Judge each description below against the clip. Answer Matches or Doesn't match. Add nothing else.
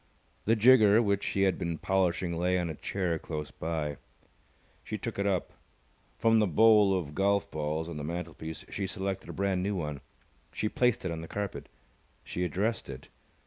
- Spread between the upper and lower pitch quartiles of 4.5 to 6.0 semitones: Doesn't match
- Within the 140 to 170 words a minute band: Doesn't match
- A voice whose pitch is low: Matches